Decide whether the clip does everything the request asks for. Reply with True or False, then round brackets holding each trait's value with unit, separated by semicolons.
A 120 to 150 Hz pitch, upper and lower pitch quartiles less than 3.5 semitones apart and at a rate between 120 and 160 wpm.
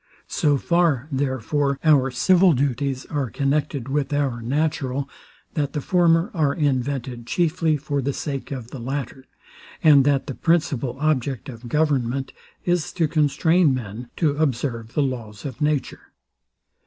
True (140 Hz; 2.8 semitones; 140 wpm)